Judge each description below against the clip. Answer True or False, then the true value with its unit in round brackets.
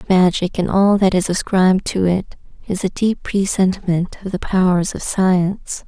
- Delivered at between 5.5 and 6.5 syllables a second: False (4.7 syllables/s)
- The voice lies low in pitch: False (185 Hz)